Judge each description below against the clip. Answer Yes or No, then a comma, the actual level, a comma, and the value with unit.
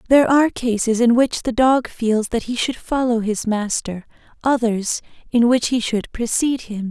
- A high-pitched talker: Yes, high, 235 Hz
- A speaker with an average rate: Yes, average, 180 wpm